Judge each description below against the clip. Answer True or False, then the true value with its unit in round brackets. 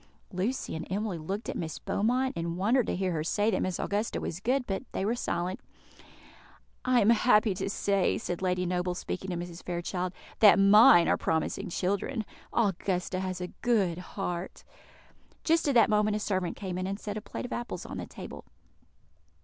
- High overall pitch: True (195 Hz)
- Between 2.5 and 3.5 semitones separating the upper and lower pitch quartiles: True (3.2 semitones)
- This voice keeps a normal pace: True (190 wpm)